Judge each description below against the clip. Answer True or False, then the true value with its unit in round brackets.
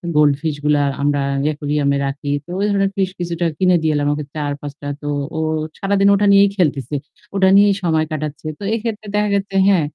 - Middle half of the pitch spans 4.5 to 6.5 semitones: True (5.1 semitones)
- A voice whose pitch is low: False (160 Hz)